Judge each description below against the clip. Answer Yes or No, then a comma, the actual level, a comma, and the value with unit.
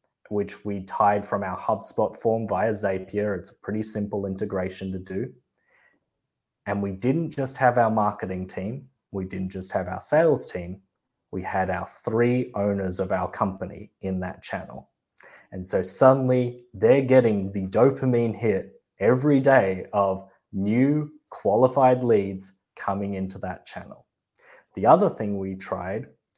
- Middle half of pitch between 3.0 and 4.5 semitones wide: Yes, average, 4.2 semitones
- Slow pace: No, average, 150 wpm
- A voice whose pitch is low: Yes, low, 100 Hz